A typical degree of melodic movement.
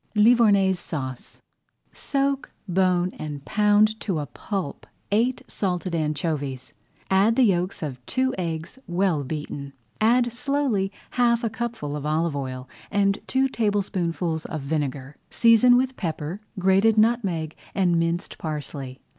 No: wide, 6.3 semitones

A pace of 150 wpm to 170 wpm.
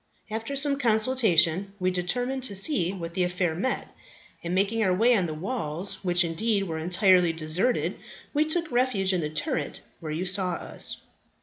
No: average, 180 wpm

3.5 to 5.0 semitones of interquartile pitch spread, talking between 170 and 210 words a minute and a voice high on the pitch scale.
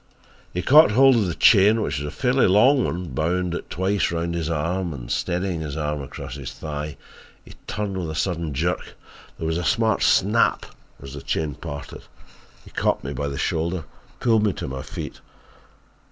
No: average, 4.6 semitones; average, 195 wpm; very low, 85 Hz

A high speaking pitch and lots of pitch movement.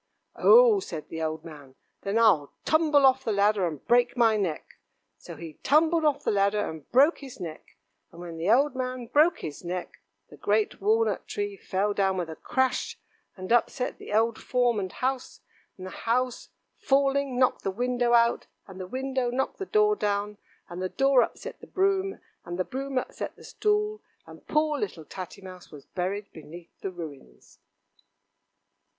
Yes: high, 230 Hz; wide, 6.9 semitones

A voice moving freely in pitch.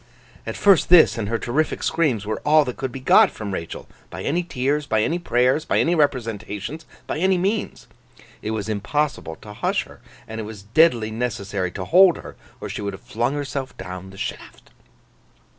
Yes: wide, 6.6 semitones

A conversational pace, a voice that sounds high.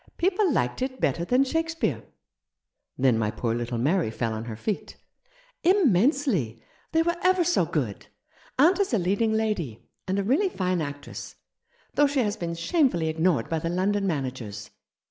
Yes: average, 175 wpm; high, 195 Hz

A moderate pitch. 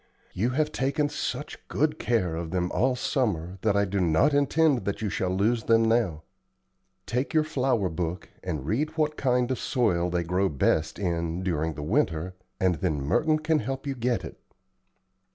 No: low, 105 Hz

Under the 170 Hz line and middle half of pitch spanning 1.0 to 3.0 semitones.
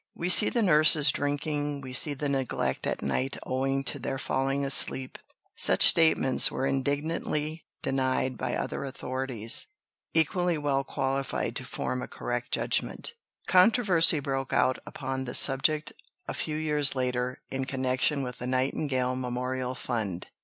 Yes: low, 135 Hz; narrow, 2.6 semitones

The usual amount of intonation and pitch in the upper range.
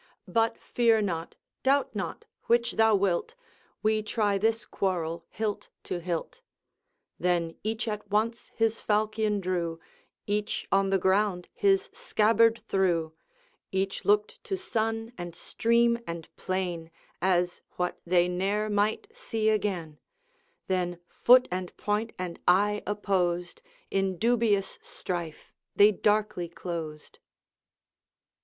Yes: average, 3.9 semitones; high, 205 Hz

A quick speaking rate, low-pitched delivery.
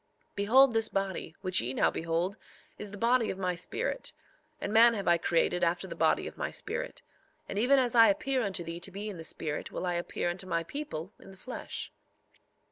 No: fast, 215 wpm; high, 195 Hz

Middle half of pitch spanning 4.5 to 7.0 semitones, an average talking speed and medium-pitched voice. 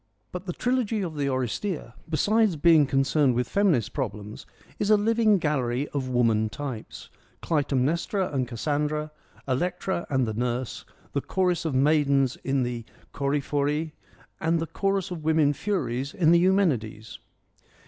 Yes: wide, 5.5 semitones; average, 150 wpm; medium, 145 Hz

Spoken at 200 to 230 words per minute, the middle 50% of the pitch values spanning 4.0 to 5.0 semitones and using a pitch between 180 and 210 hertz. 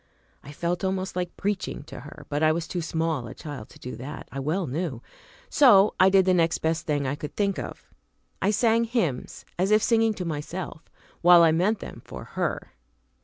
No: fast, 205 wpm; average, 4.3 semitones; medium, 170 Hz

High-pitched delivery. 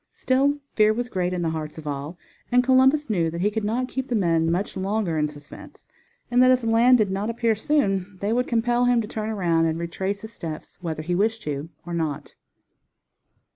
Yes: high, 205 Hz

